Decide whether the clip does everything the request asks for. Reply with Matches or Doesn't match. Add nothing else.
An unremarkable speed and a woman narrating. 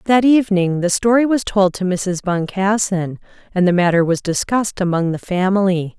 Matches